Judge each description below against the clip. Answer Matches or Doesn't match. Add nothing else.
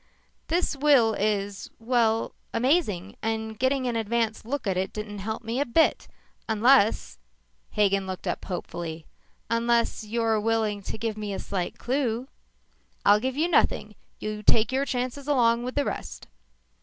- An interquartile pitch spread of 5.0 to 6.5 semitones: Doesn't match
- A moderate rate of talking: Matches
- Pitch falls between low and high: Doesn't match